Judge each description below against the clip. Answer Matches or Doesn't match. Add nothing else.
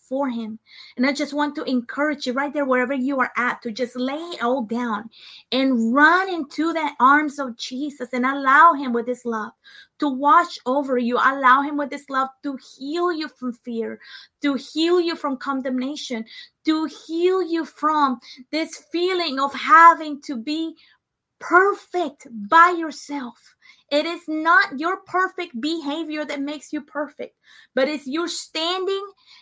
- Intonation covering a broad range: Doesn't match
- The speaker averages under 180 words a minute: Matches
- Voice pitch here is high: Matches